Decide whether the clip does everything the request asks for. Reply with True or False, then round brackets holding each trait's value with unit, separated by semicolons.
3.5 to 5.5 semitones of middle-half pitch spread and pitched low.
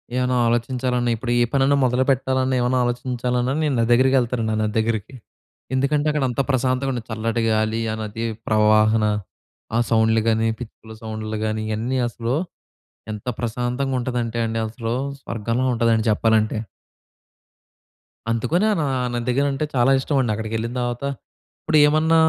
False (2.8 semitones; 120 Hz)